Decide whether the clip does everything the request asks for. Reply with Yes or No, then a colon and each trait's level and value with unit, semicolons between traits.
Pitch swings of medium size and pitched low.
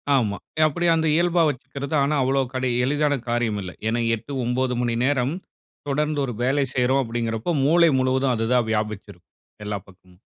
Yes: average, 4.0 semitones; low, 130 Hz